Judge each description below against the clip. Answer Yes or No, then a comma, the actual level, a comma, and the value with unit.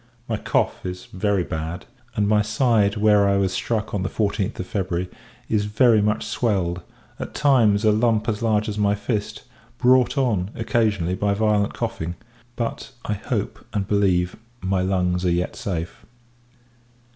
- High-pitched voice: No, low, 105 Hz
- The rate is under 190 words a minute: Yes, average, 160 wpm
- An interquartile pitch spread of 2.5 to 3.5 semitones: Yes, average, 2.8 semitones